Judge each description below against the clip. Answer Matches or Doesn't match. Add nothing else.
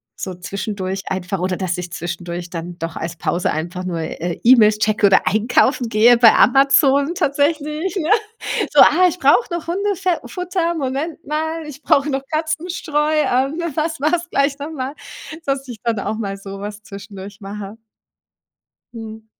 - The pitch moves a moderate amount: Doesn't match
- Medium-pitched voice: Doesn't match